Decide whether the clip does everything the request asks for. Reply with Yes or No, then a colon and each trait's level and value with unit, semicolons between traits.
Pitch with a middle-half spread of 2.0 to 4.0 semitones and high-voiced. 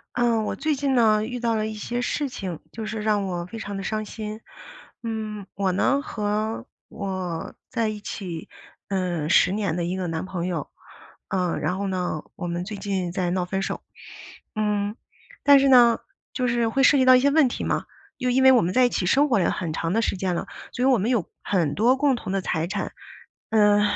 No: average, 4.5 semitones; high, 210 Hz